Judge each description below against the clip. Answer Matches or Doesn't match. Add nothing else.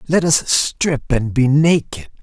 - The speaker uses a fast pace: Doesn't match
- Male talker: Matches